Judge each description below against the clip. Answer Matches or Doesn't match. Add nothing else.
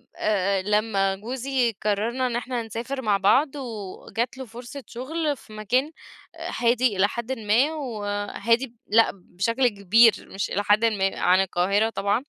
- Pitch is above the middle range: Matches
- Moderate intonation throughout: Matches